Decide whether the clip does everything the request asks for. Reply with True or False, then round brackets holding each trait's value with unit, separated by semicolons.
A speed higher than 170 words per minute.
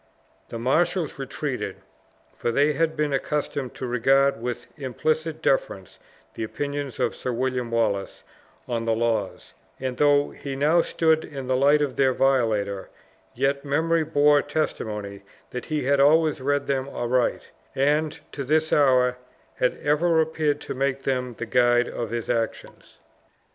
False (150 wpm)